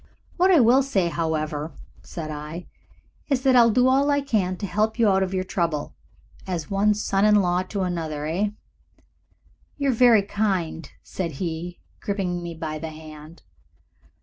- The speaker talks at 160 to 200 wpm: Yes, average, 170 wpm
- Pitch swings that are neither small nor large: Yes, average, 5.0 semitones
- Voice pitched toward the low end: No, medium, 185 Hz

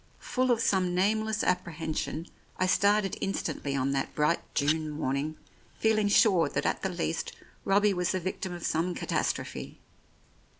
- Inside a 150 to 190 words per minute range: Yes, average, 155 wpm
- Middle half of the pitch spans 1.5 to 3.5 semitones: No, average, 4.4 semitones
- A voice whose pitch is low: No, medium, 180 Hz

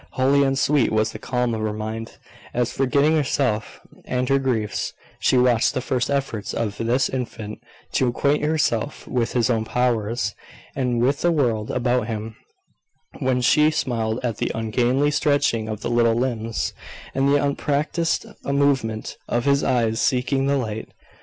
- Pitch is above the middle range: No, low, 125 Hz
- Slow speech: No, average, 160 wpm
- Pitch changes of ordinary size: Yes, average, 3.5 semitones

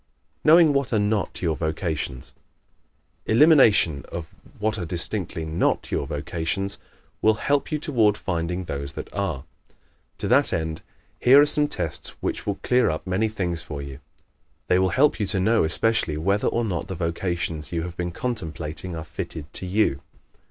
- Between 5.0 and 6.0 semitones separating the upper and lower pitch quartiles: Yes, average, 5.3 semitones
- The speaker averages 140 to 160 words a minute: No, average, 170 wpm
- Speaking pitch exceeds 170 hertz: No, very low, 90 Hz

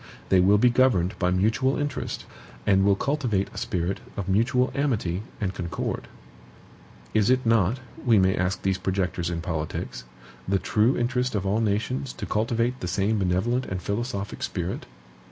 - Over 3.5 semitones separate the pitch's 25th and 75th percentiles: Yes, average, 4.5 semitones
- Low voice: Yes, low, 100 Hz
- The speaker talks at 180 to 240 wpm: No, average, 160 wpm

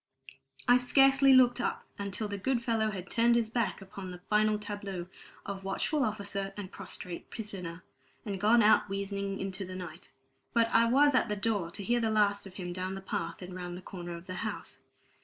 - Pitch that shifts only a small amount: No, average, 3.5 semitones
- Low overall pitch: No, high, 200 Hz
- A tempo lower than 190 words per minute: No, average, 200 wpm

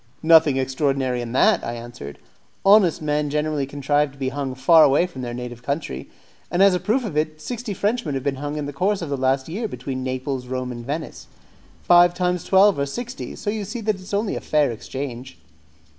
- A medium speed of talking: No, fast, 210 wpm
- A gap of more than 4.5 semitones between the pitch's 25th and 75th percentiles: Yes, wide, 5.4 semitones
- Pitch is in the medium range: Yes, medium, 145 Hz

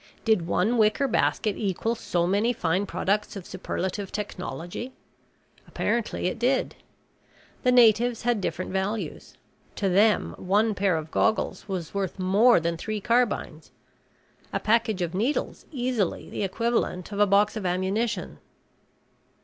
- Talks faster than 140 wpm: No, slow, 135 wpm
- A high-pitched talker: Yes, high, 205 Hz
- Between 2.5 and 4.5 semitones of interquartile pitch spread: Yes, average, 3.6 semitones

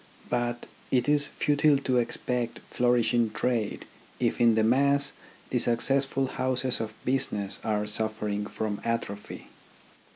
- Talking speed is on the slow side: Yes, slow, 125 wpm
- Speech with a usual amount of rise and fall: Yes, average, 3.0 semitones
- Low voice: Yes, low, 120 Hz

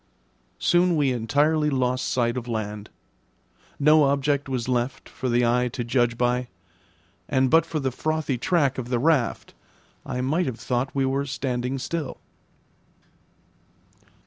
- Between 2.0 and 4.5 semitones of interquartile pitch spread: Yes, average, 3.0 semitones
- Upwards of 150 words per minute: No, average, 145 wpm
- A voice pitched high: No, low, 130 Hz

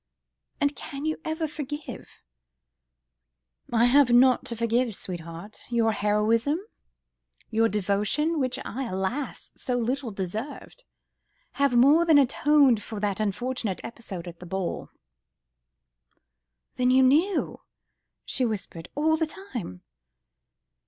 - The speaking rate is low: Yes, slow, 120 wpm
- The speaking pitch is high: Yes, high, 245 Hz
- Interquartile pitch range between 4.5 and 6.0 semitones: Yes, wide, 5.4 semitones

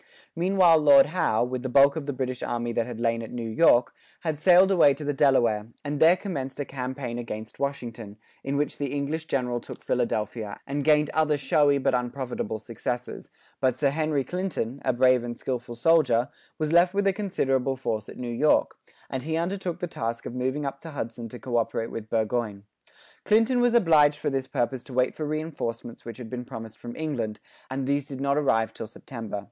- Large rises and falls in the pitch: No, average, 4.2 semitones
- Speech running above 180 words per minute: Yes, average, 200 wpm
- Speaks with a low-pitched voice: Yes, low, 130 Hz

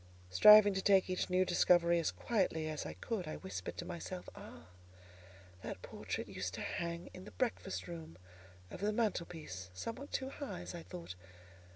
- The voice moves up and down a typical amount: Yes, average, 4.4 semitones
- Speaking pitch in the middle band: Yes, medium, 180 Hz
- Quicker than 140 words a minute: Yes, average, 180 wpm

